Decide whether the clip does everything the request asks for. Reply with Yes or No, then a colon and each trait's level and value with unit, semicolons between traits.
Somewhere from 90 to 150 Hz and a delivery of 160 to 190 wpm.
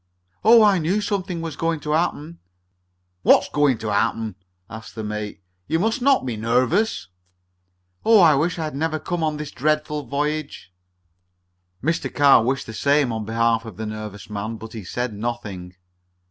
Yes: medium, 140 Hz; average, 175 wpm